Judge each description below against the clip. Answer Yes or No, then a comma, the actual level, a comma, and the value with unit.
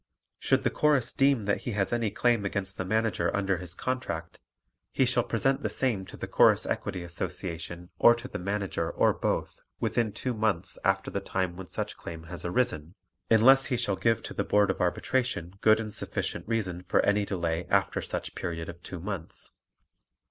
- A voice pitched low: Yes, low, 100 Hz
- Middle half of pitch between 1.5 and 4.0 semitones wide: No, average, 4.7 semitones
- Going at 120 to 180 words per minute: No, average, 190 wpm